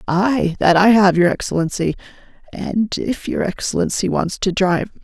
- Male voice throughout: No, female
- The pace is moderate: Yes, average, 155 wpm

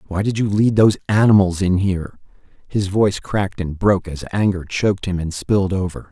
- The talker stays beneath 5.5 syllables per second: No, 5.8 syllables/s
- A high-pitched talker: No, very low, 95 Hz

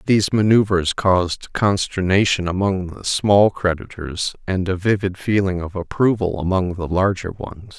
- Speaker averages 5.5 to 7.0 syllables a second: No, 4.5 syllables/s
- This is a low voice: Yes, very low, 95 Hz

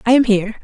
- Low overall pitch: No, high, 225 Hz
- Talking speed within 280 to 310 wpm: Yes, fast, 285 wpm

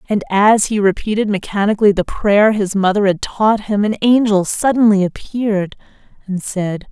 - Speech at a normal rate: Yes, average, 155 wpm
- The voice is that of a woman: Yes, female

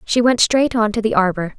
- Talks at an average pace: No, fast, 265 wpm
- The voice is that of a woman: Yes, female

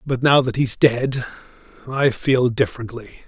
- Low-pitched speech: Yes, low, 125 Hz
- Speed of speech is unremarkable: Yes, average, 145 wpm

